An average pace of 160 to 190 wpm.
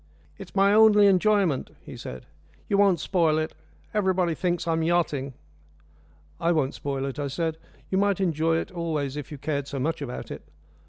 Yes: average, 175 wpm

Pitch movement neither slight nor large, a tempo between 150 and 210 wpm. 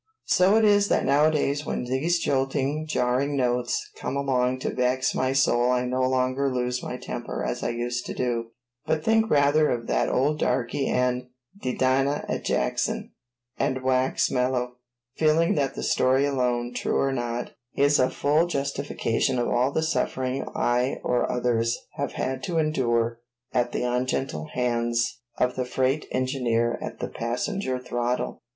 No: narrow, 2.3 semitones; average, 160 wpm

